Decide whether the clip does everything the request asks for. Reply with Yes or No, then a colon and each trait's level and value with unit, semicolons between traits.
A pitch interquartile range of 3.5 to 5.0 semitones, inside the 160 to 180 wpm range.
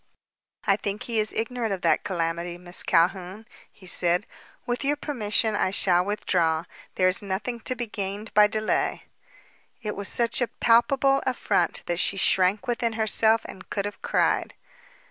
Yes: average, 3.9 semitones; average, 165 wpm